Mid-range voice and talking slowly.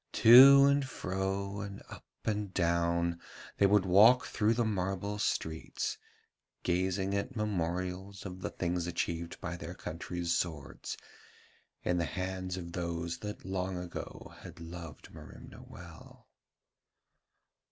No: very low, 95 Hz; slow, 125 wpm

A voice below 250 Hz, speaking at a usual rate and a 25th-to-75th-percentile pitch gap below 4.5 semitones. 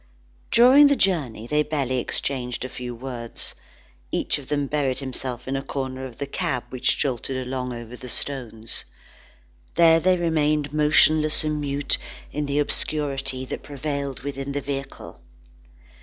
Yes: medium, 140 Hz; average, 150 wpm; narrow, 2.6 semitones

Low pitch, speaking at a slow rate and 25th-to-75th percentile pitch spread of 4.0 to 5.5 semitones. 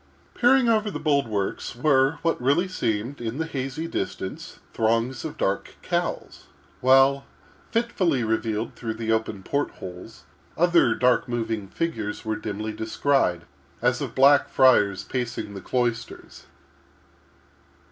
Yes: low, 125 Hz; slow, 125 wpm; average, 4.6 semitones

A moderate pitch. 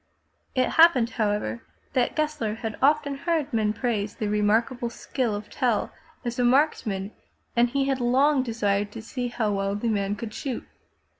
No: high, 235 Hz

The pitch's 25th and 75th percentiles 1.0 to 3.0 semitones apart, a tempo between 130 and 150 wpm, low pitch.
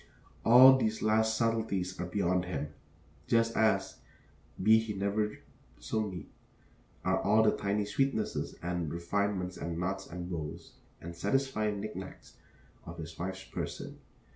No: average, 3.6 semitones; average, 140 wpm; low, 100 Hz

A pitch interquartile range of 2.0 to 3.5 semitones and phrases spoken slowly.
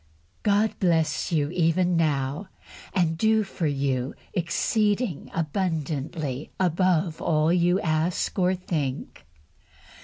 Yes: average, 3.2 semitones; slow, 100 wpm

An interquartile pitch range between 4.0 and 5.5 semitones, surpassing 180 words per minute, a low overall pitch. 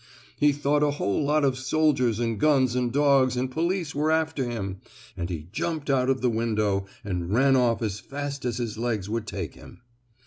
Yes: average, 4.5 semitones; average, 200 wpm; low, 125 Hz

